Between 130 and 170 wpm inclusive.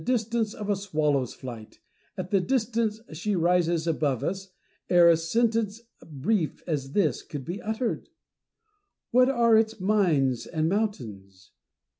Yes: average, 140 wpm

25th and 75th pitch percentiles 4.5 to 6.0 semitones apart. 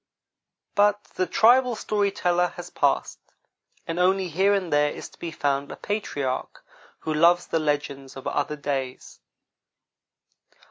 Yes: average, 5.1 semitones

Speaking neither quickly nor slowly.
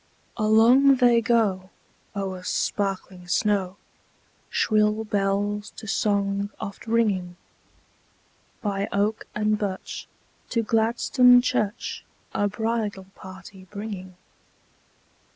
No: slow, 90 wpm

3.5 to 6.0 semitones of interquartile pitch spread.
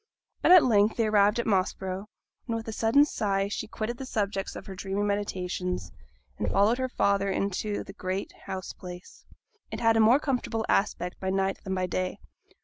No: average, 2.8 semitones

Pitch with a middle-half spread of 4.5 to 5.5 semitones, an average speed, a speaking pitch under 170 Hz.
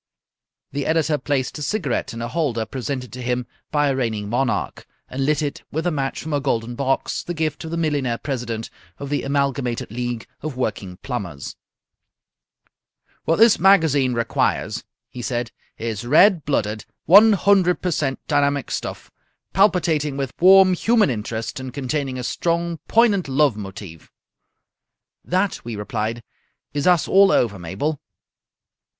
Yes: average, 5.2 semitones; average, 150 wpm; medium, 140 Hz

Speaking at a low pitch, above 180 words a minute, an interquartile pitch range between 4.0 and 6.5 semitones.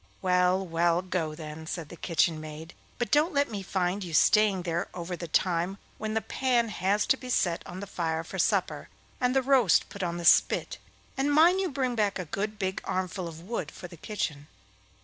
No: medium, 185 Hz; fast, 205 wpm; average, 4.4 semitones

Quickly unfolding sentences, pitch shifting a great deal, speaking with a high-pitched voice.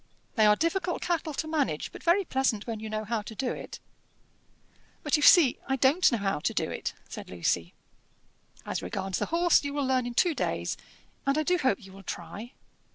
Yes: fast, 210 wpm; wide, 6.8 semitones; very high, 260 Hz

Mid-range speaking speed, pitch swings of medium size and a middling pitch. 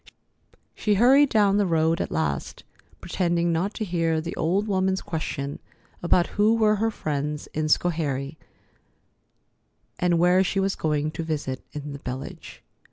Yes: average, 150 wpm; average, 4.4 semitones; medium, 170 Hz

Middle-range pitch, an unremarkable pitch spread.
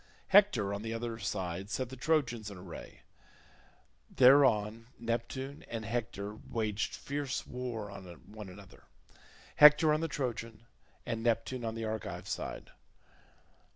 No: low, 115 Hz; average, 3.5 semitones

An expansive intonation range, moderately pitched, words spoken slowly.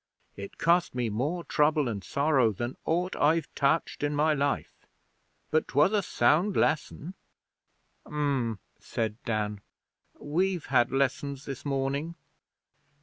No: average, 4.3 semitones; medium, 145 Hz; slow, 125 wpm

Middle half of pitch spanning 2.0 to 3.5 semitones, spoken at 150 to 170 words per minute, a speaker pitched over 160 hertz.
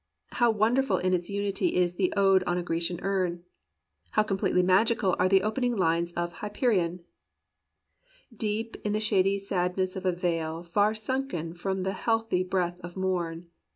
Yes: average, 3.0 semitones; average, 165 wpm; medium, 185 Hz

